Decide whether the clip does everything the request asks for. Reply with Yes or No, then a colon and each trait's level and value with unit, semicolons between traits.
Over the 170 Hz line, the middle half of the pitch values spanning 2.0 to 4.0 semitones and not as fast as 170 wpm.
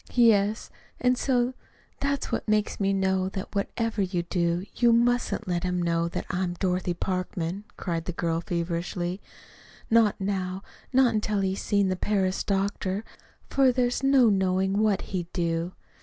Yes: high, 190 Hz; average, 3.3 semitones; average, 155 wpm